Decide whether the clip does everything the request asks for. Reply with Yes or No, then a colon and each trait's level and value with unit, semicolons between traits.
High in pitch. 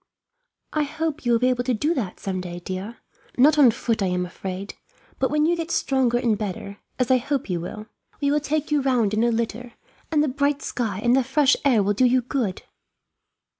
Yes: high, 245 Hz